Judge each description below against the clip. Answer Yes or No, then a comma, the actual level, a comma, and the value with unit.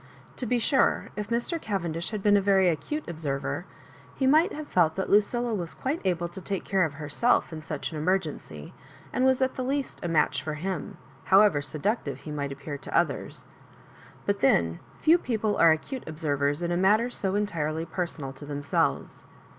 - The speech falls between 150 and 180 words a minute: No, average, 190 wpm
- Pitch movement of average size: No, wide, 6.1 semitones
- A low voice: No, medium, 180 Hz